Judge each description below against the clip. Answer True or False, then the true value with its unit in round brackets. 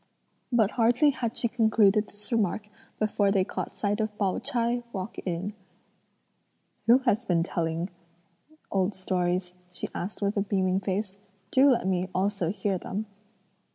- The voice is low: False (200 Hz)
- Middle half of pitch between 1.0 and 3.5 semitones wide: True (2.9 semitones)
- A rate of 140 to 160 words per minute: True (150 wpm)